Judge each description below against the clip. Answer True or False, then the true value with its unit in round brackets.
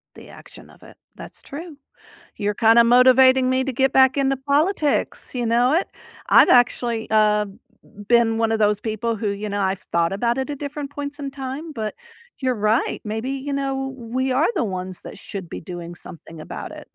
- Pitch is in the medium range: False (245 Hz)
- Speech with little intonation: False (4.2 semitones)